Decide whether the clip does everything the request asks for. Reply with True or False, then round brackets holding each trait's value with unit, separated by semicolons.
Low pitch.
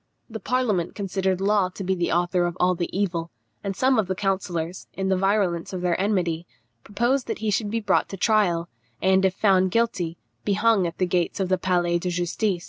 False (190 Hz)